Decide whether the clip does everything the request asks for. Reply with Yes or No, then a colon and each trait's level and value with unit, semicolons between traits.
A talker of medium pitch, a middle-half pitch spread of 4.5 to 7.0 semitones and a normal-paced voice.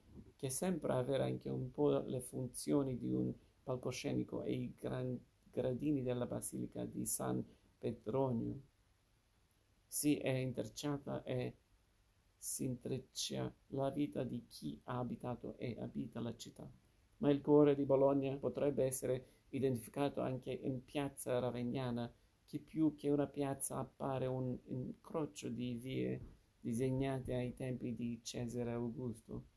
No: low, 125 Hz; average, 5.0 semitones; average, 130 wpm